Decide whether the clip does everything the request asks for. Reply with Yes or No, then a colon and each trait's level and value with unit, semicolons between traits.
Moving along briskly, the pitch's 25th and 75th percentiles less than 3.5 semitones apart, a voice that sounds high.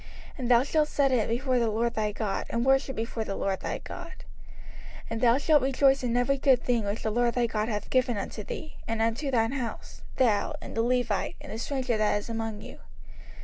Yes: fast, 225 wpm; average, 2.9 semitones; high, 235 Hz